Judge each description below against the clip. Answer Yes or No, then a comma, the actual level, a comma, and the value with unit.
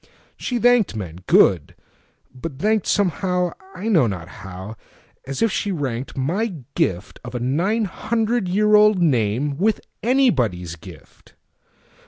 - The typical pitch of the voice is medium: Yes, medium, 165 Hz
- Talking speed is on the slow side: Yes, slow, 105 wpm